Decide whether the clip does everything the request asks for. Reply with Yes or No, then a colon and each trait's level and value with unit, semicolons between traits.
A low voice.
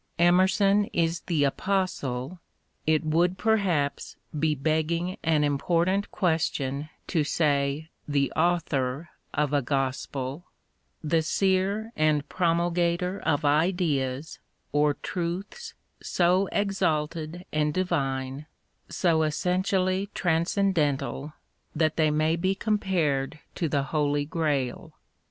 No: medium, 160 Hz